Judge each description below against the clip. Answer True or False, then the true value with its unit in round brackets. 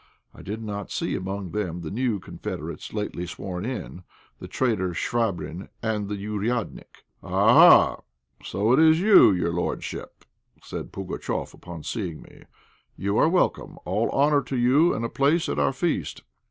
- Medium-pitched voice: False (105 Hz)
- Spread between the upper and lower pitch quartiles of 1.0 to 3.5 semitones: False (5.1 semitones)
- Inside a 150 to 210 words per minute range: True (160 wpm)